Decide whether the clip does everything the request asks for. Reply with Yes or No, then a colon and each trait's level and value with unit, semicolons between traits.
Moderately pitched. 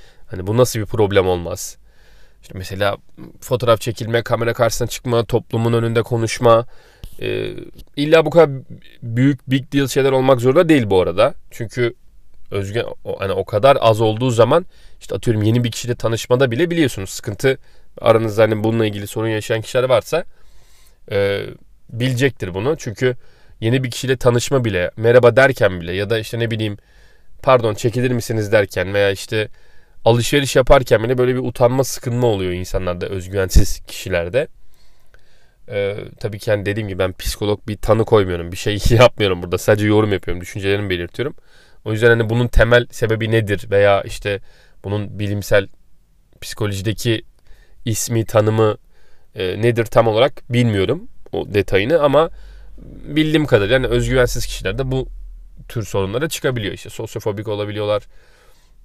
No: low, 115 Hz